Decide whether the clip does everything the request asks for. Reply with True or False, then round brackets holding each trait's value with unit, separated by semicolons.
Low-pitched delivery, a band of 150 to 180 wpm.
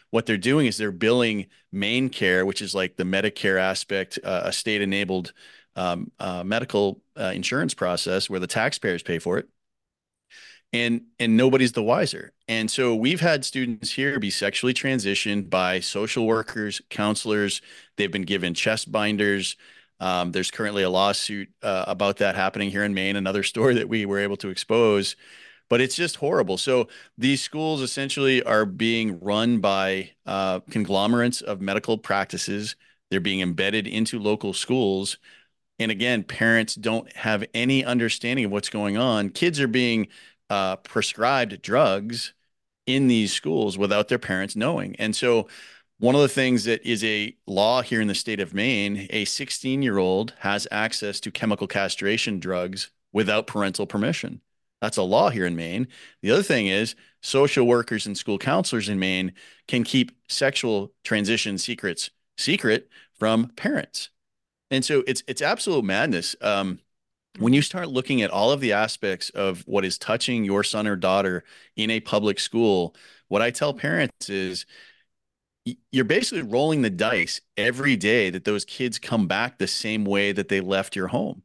True (105 Hz; 165 wpm)